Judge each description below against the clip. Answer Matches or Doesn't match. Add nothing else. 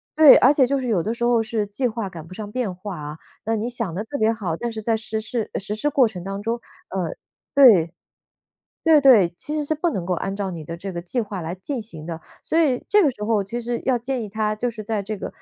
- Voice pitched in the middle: Doesn't match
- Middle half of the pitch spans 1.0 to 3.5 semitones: Doesn't match